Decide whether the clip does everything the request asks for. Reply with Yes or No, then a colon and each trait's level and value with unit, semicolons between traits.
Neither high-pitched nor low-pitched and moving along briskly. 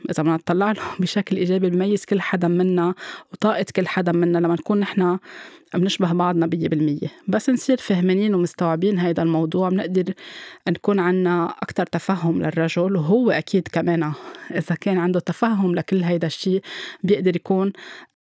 Yes: medium, 180 Hz; fast, 150 wpm